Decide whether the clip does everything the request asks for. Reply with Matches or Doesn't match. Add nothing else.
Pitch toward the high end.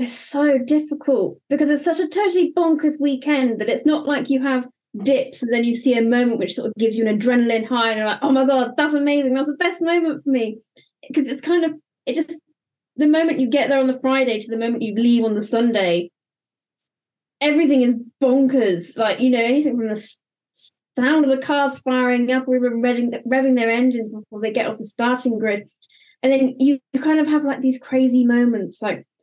Matches